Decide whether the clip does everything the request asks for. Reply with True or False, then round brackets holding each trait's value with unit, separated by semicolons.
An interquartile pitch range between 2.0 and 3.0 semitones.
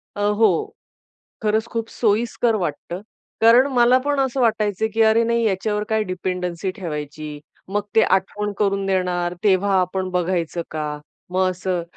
False (3.5 semitones)